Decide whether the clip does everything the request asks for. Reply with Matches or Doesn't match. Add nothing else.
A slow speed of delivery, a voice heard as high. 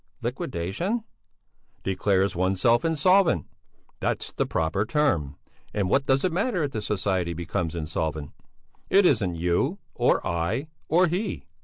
Doesn't match